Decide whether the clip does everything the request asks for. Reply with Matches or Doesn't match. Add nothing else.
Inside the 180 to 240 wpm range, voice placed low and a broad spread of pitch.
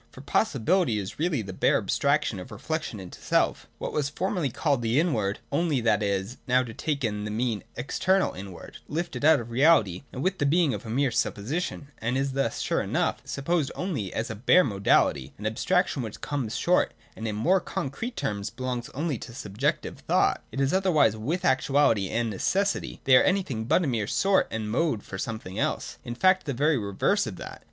Matches